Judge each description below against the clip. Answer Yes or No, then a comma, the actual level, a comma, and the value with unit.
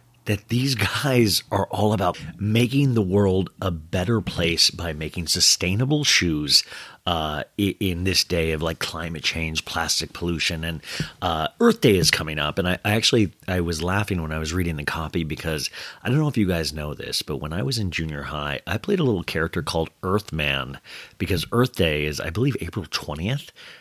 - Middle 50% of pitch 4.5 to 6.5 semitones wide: Yes, average, 4.8 semitones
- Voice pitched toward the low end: Yes, very low, 90 Hz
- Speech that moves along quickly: No, average, 195 wpm